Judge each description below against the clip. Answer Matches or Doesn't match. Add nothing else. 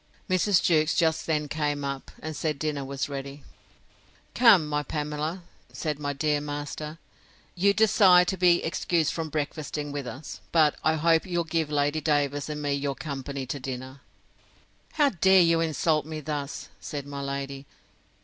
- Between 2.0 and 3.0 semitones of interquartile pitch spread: Matches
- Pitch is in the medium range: Matches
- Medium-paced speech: Matches